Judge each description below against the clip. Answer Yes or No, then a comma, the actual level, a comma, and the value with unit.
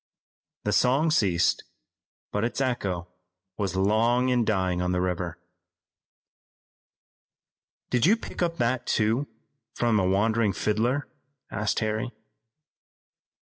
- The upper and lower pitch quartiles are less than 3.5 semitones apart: No, average, 4.6 semitones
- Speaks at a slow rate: Yes, slow, 110 wpm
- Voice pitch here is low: Yes, low, 110 Hz